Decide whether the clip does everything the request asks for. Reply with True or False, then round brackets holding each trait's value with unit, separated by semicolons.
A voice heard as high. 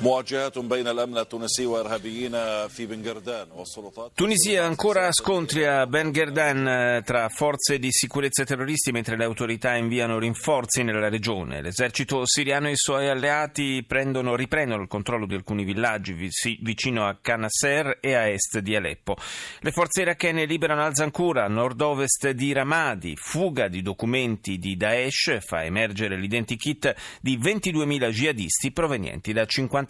False (125 Hz)